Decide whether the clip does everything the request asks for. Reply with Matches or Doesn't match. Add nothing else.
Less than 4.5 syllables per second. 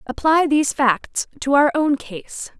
Matches